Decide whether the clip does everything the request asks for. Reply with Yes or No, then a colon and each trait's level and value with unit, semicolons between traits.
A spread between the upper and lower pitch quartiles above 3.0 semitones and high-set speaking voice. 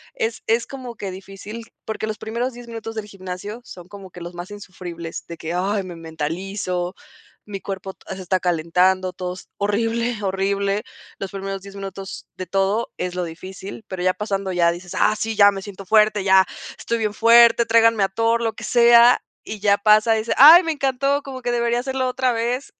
Yes: average, 3.6 semitones; high, 200 Hz